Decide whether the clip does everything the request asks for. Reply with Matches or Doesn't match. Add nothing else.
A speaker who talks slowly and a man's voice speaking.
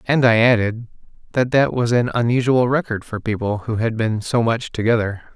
Doesn't match